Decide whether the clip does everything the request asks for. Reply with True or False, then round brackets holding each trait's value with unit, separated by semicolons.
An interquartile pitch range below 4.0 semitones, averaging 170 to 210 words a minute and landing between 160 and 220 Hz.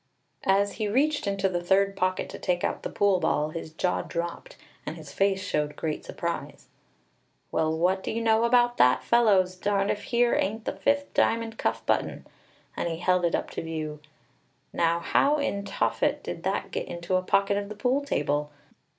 False (4.4 semitones; 190 wpm; 190 Hz)